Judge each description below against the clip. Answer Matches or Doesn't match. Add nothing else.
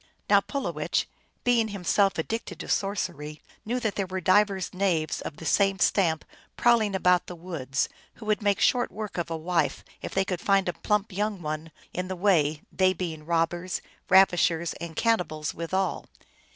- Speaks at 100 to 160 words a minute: Doesn't match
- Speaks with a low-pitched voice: Doesn't match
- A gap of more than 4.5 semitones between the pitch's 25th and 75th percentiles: Doesn't match